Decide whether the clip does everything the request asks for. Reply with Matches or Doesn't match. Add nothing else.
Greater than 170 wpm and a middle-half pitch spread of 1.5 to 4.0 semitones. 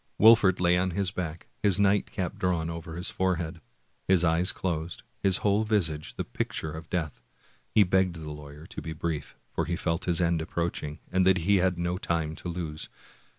Matches